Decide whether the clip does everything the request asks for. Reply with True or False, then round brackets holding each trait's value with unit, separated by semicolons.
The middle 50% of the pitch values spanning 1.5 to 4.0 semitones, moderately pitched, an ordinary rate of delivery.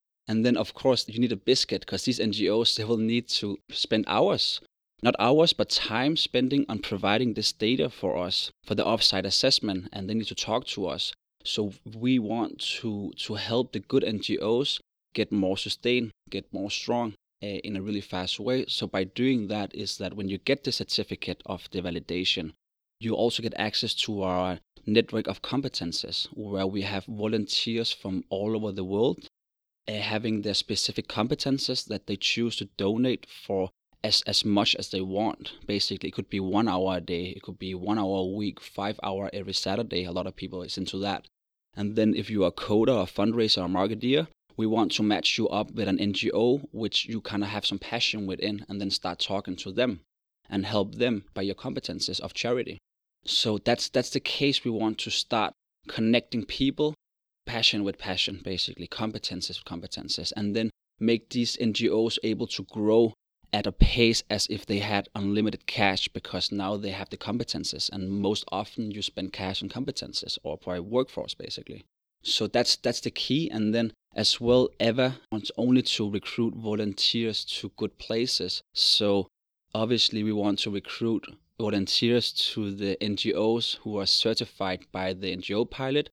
False (2.9 semitones; 105 Hz; 185 wpm)